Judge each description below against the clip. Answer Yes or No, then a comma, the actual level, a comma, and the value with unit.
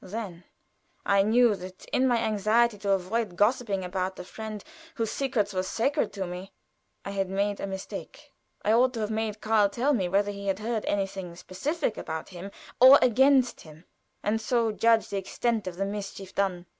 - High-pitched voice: Yes, high, 205 Hz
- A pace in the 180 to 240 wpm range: Yes, average, 185 wpm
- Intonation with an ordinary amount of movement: Yes, average, 3.1 semitones